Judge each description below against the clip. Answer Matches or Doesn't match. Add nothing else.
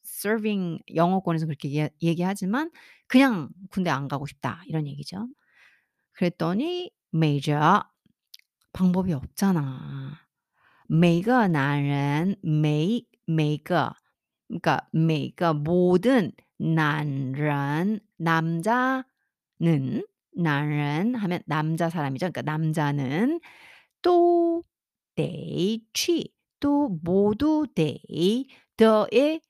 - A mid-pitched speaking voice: Matches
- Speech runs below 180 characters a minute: Matches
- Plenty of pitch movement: Matches